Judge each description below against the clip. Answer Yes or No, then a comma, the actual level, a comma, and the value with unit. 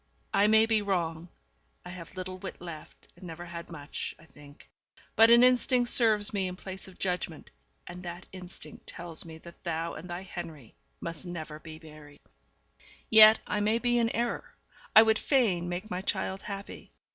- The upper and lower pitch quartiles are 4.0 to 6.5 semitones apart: Yes, average, 4.3 semitones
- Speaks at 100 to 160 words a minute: No, average, 180 wpm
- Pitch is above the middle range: No, medium, 180 Hz